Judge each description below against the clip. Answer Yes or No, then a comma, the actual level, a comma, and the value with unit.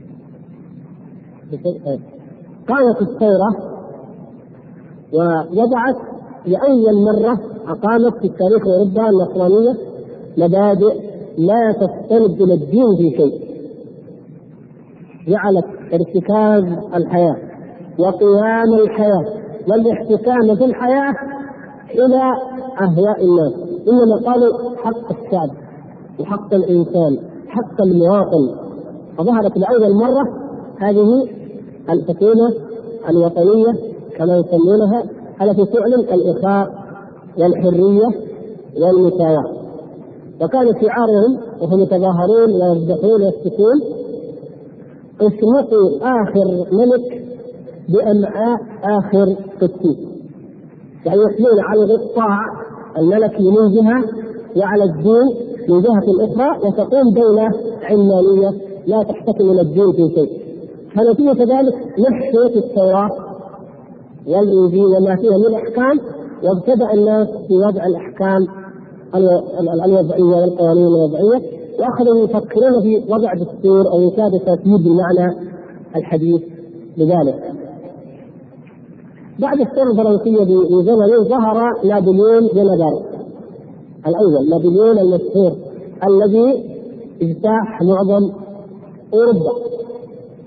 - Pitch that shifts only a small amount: No, average, 3.8 semitones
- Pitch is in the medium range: No, high, 205 Hz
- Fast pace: No, average, 85 wpm